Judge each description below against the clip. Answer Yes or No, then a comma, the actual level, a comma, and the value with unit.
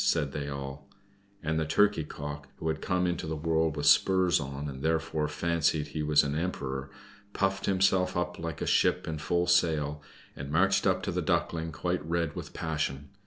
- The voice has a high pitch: No, very low, 80 Hz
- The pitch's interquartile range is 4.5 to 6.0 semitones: No, average, 3.1 semitones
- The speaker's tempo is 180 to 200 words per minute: Yes, average, 190 wpm